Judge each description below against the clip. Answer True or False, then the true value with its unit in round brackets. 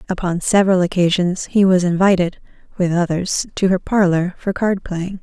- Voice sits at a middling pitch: True (180 Hz)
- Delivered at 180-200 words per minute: False (160 wpm)